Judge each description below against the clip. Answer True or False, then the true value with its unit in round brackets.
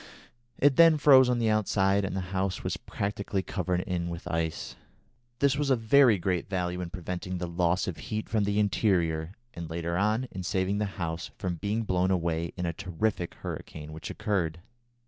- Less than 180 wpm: False (185 wpm)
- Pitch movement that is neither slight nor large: True (3.7 semitones)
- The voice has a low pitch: True (95 Hz)